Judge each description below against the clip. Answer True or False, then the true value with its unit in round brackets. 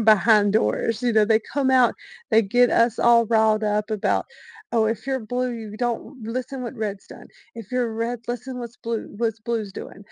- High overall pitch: True (230 Hz)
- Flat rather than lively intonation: True (2.1 semitones)